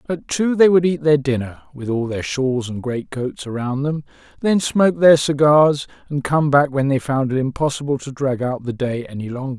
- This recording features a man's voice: Yes, male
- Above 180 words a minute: Yes, average, 200 wpm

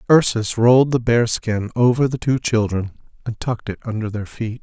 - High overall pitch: No, low, 115 Hz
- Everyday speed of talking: Yes, average, 195 wpm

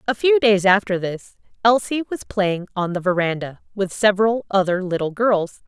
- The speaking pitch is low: No, high, 200 Hz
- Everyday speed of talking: Yes, average, 170 wpm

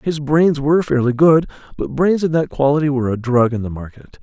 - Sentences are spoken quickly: Yes, fast, 225 wpm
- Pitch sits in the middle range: Yes, medium, 145 Hz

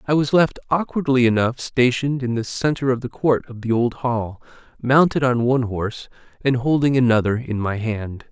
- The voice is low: Yes, low, 125 Hz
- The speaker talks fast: No, average, 190 wpm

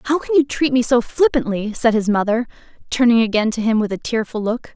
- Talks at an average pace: No, fast, 225 wpm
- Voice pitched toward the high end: Yes, high, 235 Hz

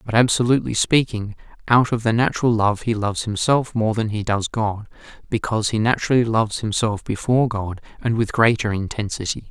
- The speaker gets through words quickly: No, average, 170 wpm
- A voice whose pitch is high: No, low, 110 Hz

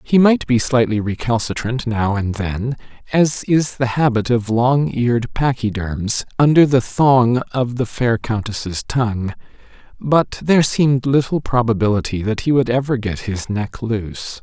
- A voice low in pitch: Yes, low, 120 Hz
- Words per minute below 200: Yes, average, 155 wpm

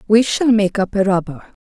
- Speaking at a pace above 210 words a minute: Yes, fast, 220 wpm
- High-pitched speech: Yes, high, 200 Hz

